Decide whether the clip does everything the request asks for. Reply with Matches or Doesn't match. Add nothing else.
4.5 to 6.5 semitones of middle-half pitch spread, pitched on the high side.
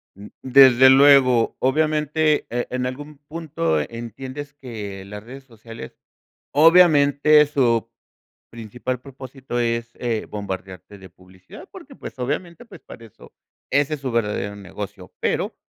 Doesn't match